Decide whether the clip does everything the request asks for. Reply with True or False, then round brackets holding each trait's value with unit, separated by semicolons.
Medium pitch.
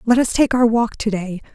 False (225 Hz)